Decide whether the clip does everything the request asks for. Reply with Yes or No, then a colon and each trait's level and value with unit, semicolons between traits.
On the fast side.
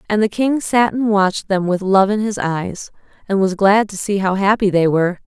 Yes: fast, 240 wpm